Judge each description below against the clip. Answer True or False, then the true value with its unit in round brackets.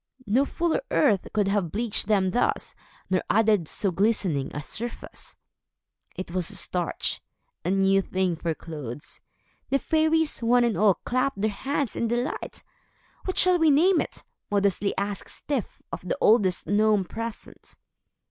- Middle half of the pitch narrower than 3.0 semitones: False (4.7 semitones)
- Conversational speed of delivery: True (150 wpm)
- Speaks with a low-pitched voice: False (210 Hz)